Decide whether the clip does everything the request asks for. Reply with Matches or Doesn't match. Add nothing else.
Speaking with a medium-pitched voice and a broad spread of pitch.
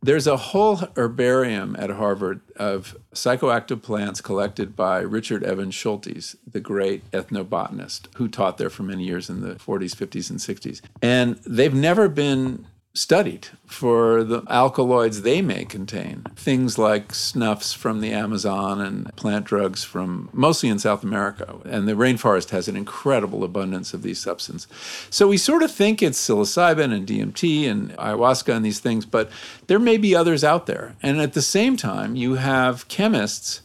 Doesn't match